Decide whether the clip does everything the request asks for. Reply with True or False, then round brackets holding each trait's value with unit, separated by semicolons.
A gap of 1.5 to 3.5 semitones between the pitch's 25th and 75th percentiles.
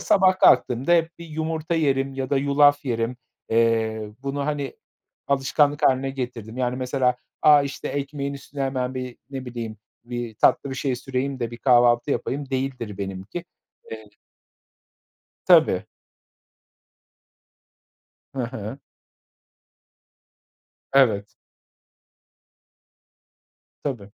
True (2.8 semitones)